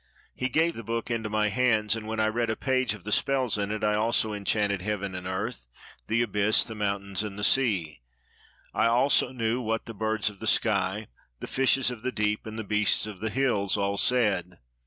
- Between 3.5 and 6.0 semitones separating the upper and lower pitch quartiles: No, narrow, 2.4 semitones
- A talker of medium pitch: No, low, 110 Hz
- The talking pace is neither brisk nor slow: No, fast, 215 wpm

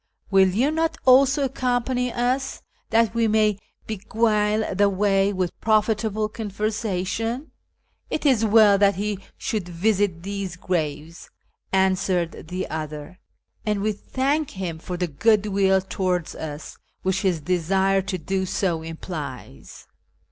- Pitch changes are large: No, average, 3.4 semitones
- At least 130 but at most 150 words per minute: Yes, average, 140 wpm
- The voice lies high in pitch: Yes, high, 200 Hz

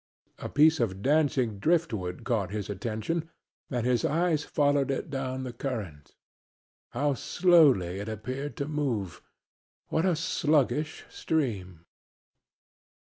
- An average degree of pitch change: No, wide, 6.1 semitones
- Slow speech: Yes, slow, 120 wpm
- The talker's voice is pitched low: Yes, low, 130 Hz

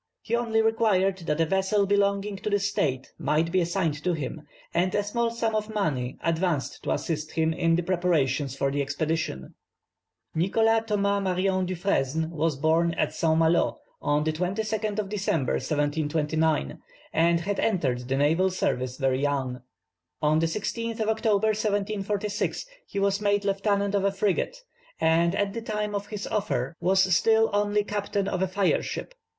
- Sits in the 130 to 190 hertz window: Yes, medium, 185 Hz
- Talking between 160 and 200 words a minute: Yes, average, 165 wpm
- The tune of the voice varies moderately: Yes, average, 4.5 semitones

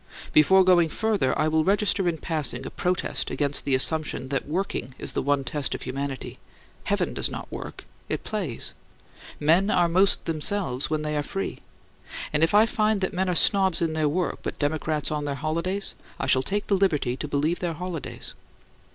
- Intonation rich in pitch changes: No, average, 4.3 semitones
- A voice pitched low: No, medium, 160 Hz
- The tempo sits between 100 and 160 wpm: No, average, 190 wpm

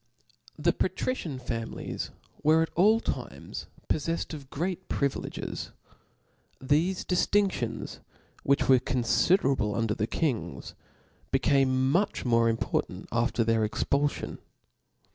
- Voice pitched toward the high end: No, medium, 140 Hz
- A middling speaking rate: No, slow, 105 wpm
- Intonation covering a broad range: Yes, wide, 6.1 semitones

